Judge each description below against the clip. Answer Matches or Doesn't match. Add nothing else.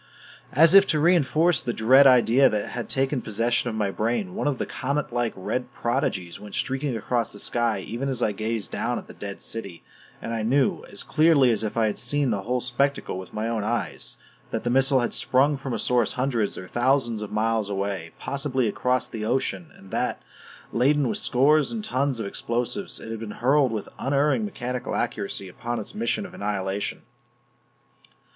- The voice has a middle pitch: Doesn't match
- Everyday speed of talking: Matches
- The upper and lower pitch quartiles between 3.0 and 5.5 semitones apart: Matches